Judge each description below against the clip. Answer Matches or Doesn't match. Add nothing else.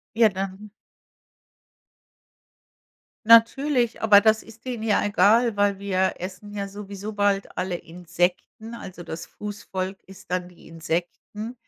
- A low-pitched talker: Doesn't match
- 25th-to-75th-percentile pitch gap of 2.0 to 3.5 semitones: Matches